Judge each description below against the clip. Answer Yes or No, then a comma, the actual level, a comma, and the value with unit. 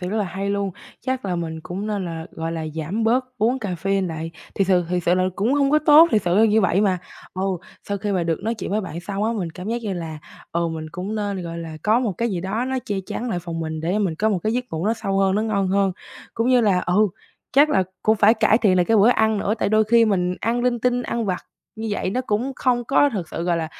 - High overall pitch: Yes, high, 200 Hz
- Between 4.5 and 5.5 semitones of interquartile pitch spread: No, average, 3.9 semitones